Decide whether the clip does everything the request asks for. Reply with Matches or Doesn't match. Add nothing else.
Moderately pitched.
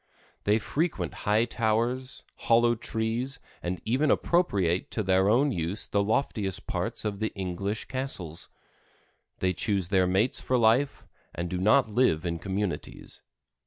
Doesn't match